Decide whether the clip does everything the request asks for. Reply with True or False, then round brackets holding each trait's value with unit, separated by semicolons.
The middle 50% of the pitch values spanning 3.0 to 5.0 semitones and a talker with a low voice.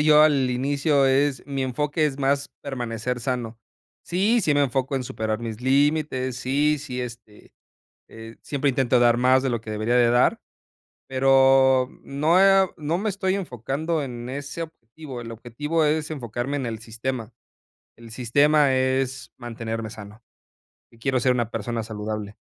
True (3.5 semitones; 130 Hz)